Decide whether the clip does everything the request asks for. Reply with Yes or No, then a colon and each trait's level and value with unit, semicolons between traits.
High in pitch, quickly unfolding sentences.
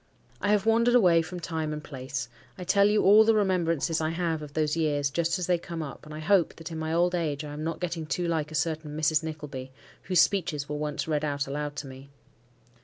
No: medium, 160 Hz; fast, 240 wpm